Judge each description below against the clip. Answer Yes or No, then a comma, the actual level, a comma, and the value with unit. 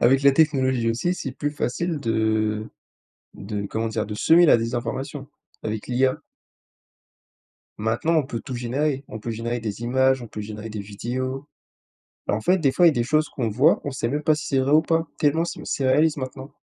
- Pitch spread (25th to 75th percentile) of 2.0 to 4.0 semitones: No, average, 4.5 semitones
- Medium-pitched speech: No, low, 130 Hz